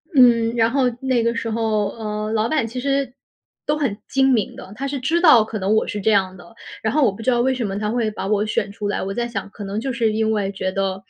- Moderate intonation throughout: Yes, average, 3.3 semitones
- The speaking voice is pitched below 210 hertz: No, high, 225 Hz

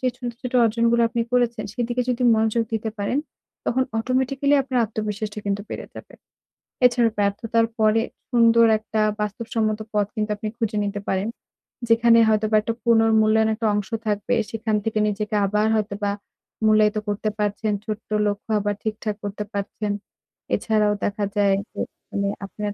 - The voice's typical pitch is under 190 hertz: No, high, 215 Hz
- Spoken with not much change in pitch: Yes, narrow, 1.9 semitones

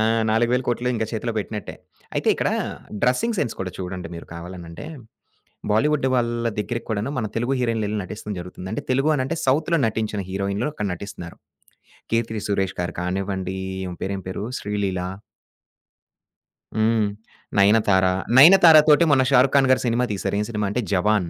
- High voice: No, low, 110 Hz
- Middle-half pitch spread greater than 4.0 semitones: Yes, average, 4.5 semitones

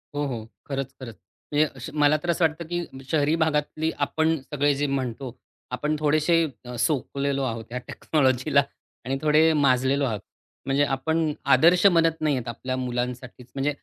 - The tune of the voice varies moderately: Yes, average, 3.3 semitones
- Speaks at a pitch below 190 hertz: Yes, medium, 140 Hz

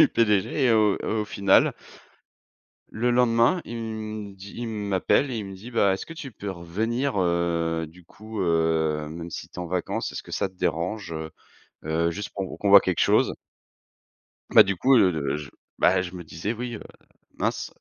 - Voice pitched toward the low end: Yes, low, 100 Hz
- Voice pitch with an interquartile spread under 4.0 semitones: No, average, 4.5 semitones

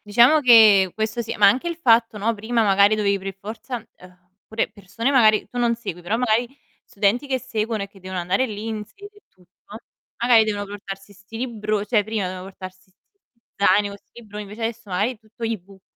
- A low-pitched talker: No, high, 215 Hz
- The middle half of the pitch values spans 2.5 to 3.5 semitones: Yes, average, 2.8 semitones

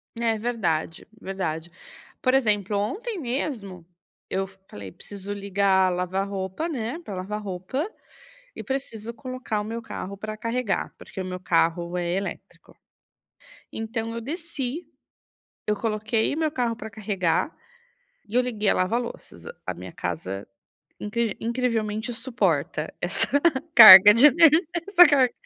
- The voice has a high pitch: Yes, high, 215 Hz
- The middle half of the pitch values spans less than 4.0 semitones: No, average, 4.6 semitones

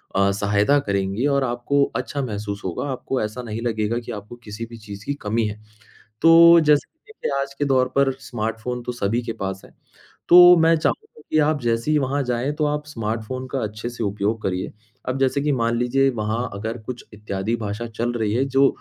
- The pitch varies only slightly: No, average, 4.3 semitones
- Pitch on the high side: No, low, 120 Hz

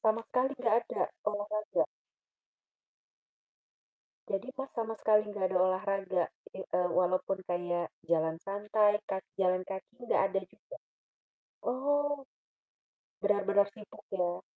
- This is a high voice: Yes, high, 200 Hz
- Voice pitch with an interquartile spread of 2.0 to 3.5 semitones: Yes, average, 2.8 semitones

